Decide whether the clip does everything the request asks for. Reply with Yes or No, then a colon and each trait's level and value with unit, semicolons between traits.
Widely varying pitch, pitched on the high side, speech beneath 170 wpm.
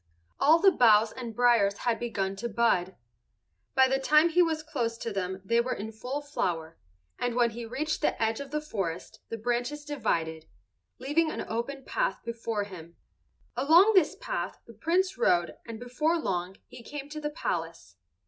No: wide, 6.4 semitones; high, 240 Hz; average, 175 wpm